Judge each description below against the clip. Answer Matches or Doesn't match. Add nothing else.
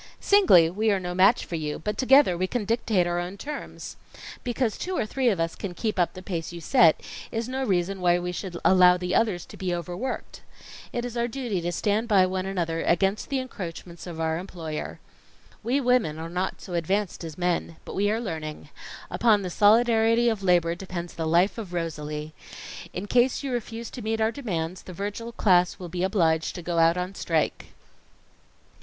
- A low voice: Doesn't match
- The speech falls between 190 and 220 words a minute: Matches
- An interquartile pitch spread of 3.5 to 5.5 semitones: Matches